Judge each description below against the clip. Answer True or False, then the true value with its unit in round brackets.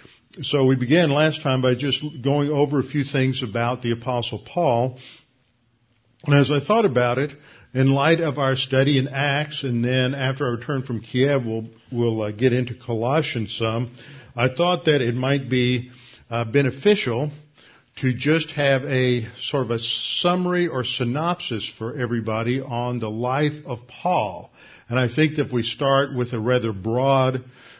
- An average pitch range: True (3.1 semitones)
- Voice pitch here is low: True (130 Hz)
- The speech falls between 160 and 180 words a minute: True (170 wpm)